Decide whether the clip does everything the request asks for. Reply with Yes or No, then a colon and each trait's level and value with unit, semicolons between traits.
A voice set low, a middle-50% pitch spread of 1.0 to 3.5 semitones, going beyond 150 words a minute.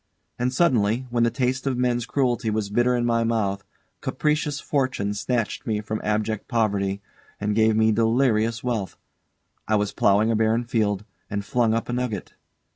Yes: low, 115 Hz; average, 2.7 semitones; average, 170 wpm